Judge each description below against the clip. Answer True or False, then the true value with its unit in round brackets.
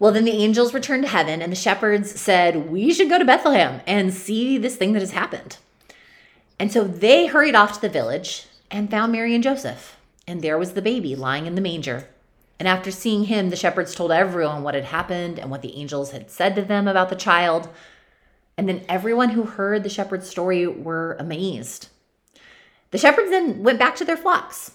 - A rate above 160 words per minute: True (205 wpm)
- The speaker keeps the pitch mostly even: False (4.6 semitones)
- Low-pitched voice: False (190 Hz)